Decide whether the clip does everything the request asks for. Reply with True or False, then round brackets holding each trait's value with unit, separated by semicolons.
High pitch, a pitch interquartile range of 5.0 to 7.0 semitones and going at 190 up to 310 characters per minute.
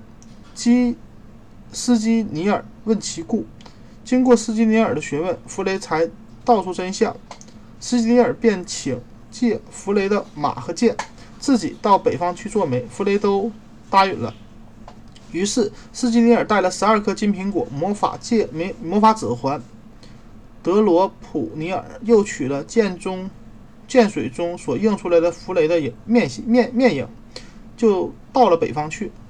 True (200 Hz; 5.4 semitones; 215 characters per minute)